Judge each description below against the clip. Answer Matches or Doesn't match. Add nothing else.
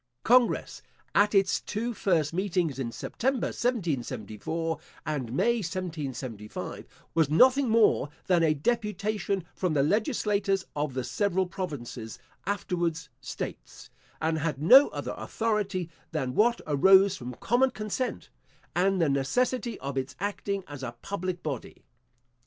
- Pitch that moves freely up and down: Matches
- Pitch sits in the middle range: Matches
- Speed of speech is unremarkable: Doesn't match